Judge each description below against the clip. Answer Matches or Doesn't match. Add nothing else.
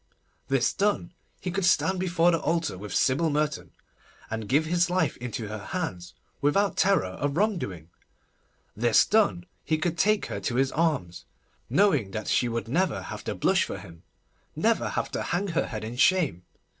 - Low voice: Doesn't match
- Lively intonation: Matches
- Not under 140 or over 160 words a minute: Doesn't match